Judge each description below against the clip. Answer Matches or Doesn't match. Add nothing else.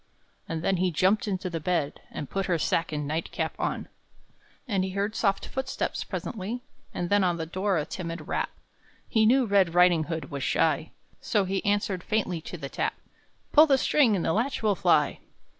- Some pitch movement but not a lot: Matches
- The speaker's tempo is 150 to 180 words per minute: Doesn't match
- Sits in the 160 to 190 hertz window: Matches